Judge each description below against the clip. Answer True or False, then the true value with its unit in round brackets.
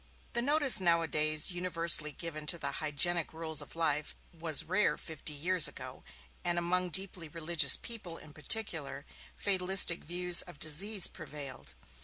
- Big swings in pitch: False (2.9 semitones)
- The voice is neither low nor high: True (170 Hz)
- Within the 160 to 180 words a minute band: False (140 wpm)